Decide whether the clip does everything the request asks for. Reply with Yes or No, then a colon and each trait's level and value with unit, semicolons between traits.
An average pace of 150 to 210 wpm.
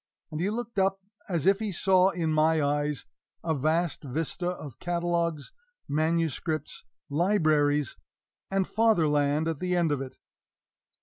No: slow, 135 wpm